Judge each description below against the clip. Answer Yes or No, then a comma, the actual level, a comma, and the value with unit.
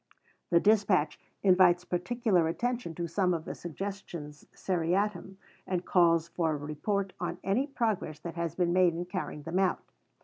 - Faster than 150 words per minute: Yes, average, 160 wpm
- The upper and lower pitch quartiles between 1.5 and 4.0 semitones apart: Yes, average, 2.8 semitones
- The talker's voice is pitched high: No, medium, 180 Hz